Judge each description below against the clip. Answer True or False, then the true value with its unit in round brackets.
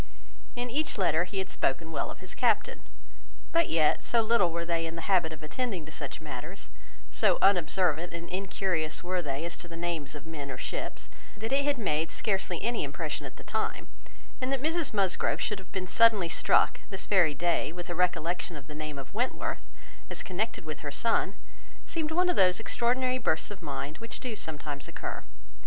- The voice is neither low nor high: True (180 Hz)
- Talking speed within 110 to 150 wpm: False (200 wpm)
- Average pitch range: False (6.0 semitones)